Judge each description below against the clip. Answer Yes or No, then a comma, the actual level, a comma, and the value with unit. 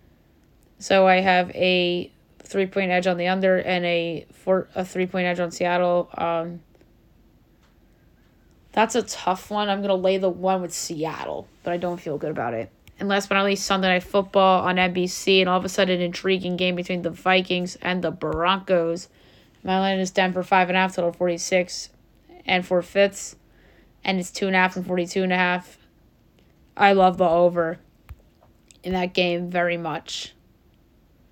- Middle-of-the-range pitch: Yes, medium, 180 Hz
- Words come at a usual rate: Yes, average, 185 wpm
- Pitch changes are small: Yes, narrow, 1.3 semitones